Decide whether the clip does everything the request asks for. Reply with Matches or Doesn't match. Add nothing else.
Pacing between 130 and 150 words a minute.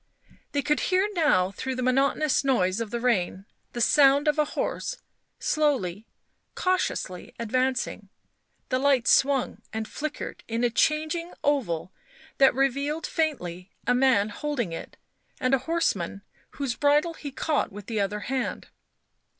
Matches